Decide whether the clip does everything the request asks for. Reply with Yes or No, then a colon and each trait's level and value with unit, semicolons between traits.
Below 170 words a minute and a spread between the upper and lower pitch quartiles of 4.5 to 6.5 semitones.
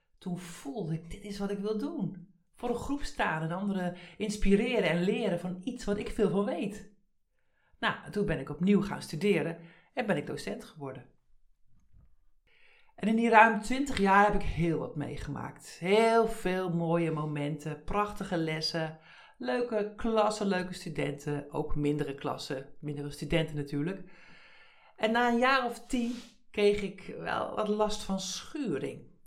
Yes: average, 160 wpm; average, 5.0 semitones